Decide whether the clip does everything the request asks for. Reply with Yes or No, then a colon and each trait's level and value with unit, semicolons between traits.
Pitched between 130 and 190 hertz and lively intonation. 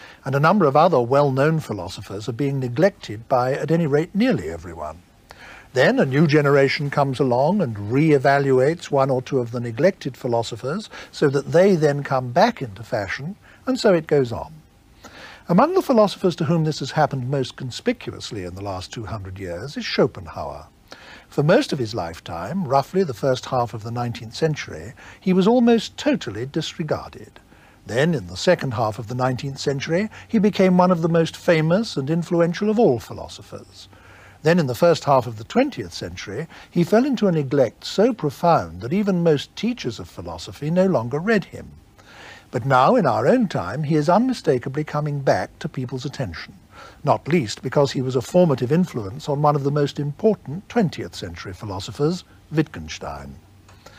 Yes: medium, 140 Hz; wide, 6.3 semitones